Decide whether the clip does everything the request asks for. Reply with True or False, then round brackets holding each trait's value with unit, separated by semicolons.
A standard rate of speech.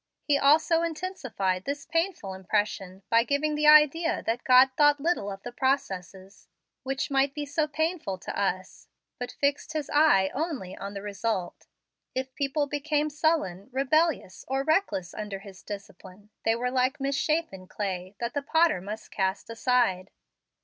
True (155 wpm)